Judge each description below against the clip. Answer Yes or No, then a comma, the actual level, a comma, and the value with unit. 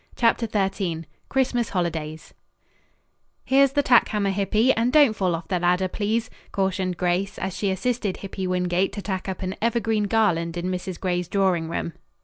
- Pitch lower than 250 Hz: Yes, high, 190 Hz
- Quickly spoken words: No, average, 165 wpm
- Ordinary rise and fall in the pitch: Yes, average, 3.6 semitones